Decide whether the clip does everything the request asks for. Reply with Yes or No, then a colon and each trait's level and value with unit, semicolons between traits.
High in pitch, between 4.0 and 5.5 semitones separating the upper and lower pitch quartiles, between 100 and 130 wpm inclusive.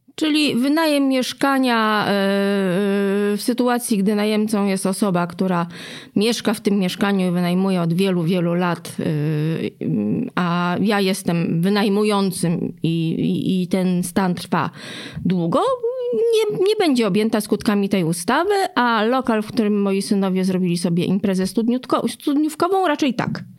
Yes: high, 205 Hz; average, 4.8 semitones; average, 125 wpm